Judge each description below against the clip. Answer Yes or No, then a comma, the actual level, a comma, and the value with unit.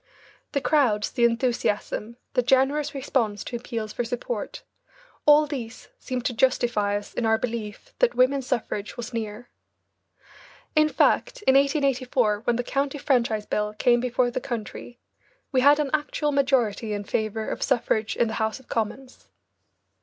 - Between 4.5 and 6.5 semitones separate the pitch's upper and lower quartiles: No, average, 3.6 semitones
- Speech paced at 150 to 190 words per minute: Yes, average, 155 wpm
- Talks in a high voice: Yes, high, 245 Hz